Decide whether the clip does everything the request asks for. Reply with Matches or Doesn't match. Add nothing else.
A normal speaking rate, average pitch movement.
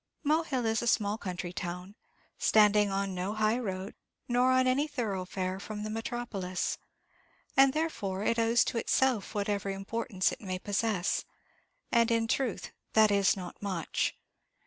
Matches